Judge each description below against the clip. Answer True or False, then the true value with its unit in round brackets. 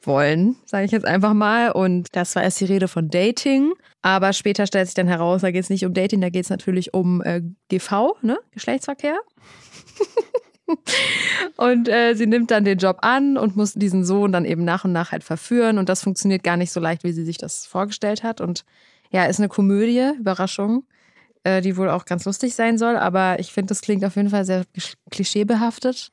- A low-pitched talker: False (200 Hz)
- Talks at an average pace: False (210 wpm)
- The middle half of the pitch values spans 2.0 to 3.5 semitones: False (3.9 semitones)